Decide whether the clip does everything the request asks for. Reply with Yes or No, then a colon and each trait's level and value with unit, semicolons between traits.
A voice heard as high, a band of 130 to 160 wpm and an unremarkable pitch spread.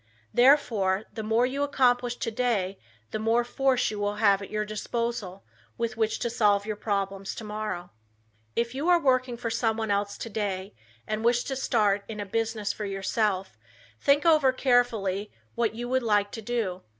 No: high, 220 Hz; average, 170 wpm; average, 3.1 semitones